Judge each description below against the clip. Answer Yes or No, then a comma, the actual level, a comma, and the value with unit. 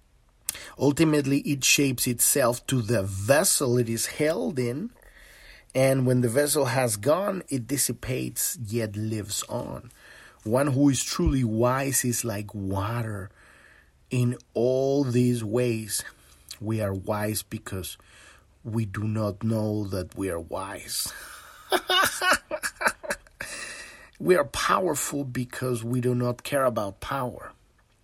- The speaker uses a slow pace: Yes, slow, 120 wpm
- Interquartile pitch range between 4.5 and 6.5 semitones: No, average, 3.7 semitones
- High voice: No, low, 120 Hz